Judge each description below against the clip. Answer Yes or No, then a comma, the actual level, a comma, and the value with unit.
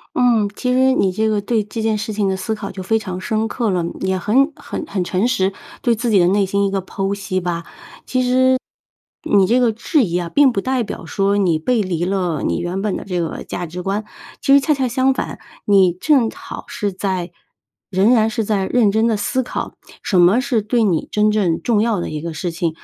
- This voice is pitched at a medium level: No, high, 205 Hz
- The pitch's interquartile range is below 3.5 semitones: No, average, 3.8 semitones